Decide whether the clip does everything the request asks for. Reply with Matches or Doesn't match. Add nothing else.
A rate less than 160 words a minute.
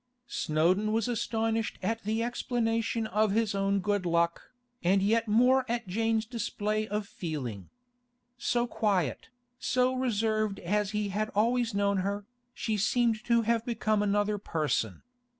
Matches